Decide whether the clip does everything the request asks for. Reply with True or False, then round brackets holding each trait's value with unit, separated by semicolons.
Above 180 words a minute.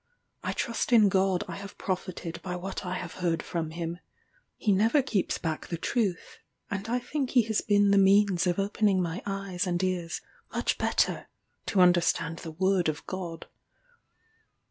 False (170 wpm)